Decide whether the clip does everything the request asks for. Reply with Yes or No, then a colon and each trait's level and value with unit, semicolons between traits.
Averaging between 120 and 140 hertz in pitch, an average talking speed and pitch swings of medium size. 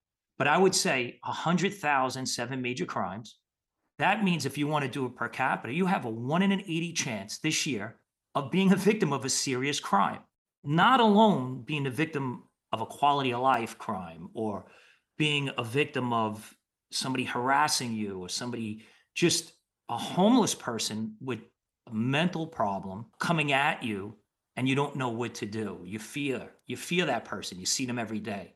Yes: low, 135 Hz; average, 180 wpm; average, 5.0 semitones